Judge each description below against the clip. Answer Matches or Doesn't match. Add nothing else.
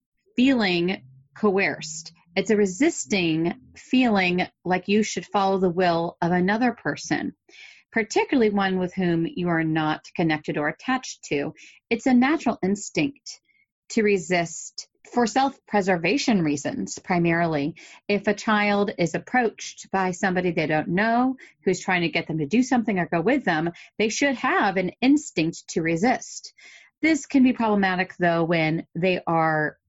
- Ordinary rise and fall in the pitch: Doesn't match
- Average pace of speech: Matches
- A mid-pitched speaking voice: Doesn't match